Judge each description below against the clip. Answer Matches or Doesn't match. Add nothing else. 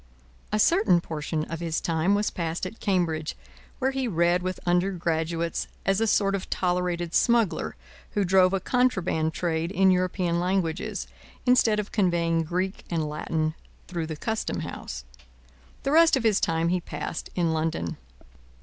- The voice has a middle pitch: Matches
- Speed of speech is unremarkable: Matches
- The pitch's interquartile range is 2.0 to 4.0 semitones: Matches